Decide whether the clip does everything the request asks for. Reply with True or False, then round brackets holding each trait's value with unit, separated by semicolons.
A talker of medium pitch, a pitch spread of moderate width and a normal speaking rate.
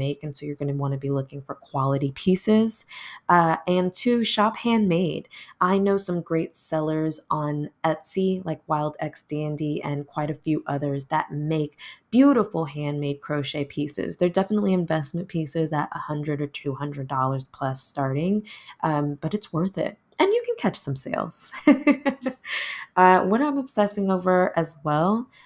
True (160 Hz; 4.9 semitones; 165 wpm)